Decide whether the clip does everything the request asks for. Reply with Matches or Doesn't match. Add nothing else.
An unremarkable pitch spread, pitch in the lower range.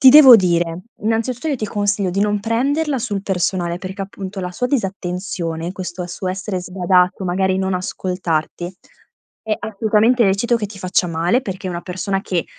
Doesn't match